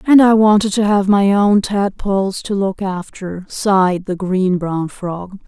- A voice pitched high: Yes, high, 195 Hz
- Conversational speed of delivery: Yes, average, 175 wpm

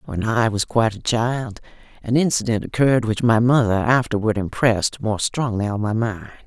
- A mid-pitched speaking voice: No, low, 115 Hz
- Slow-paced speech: No, average, 175 wpm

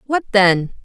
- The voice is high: Yes, high, 215 Hz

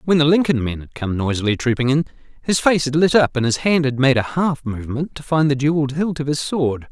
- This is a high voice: No, medium, 140 Hz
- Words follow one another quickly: Yes, fast, 260 wpm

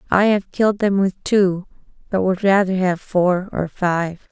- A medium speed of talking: Yes, average, 180 wpm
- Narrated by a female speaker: Yes, female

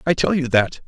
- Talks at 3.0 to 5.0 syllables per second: No, 5.5 syllables/s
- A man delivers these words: Yes, male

